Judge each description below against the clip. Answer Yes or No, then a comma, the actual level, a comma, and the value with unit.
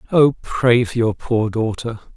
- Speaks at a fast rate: No, average, 165 wpm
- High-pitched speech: No, low, 115 Hz